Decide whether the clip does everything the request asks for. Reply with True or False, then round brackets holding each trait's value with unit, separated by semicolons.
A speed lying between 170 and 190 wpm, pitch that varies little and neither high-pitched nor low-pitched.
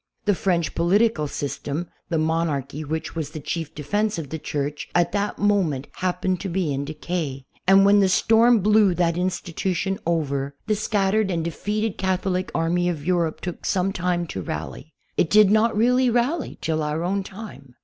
False (180 wpm; 4.3 semitones; 180 Hz)